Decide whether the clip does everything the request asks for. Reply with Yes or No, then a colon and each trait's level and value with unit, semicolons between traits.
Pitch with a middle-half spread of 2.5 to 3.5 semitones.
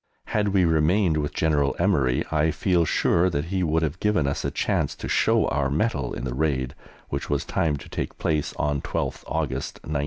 Yes: average, 2.9 semitones